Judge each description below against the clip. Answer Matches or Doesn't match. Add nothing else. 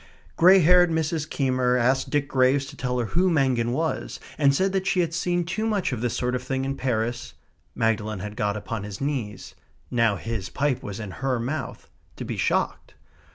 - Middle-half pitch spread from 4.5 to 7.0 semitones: Matches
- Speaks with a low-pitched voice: Matches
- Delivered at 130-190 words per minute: Doesn't match